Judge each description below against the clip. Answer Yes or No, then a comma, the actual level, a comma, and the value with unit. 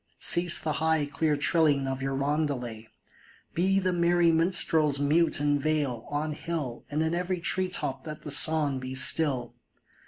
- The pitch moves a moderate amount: Yes, average, 3.1 semitones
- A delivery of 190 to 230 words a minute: No, average, 160 wpm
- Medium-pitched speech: Yes, medium, 150 Hz